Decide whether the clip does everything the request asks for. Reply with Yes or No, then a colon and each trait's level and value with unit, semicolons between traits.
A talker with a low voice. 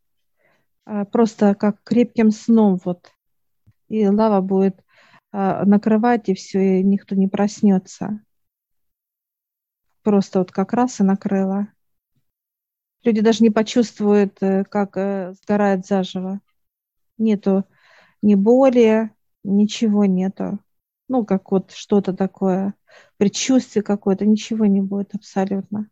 No: high, 200 Hz